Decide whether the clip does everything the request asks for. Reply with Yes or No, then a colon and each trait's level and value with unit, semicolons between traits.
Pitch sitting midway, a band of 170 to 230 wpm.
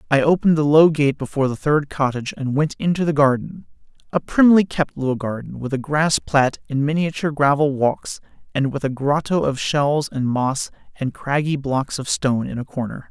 Yes: medium, 145 Hz; average, 190 wpm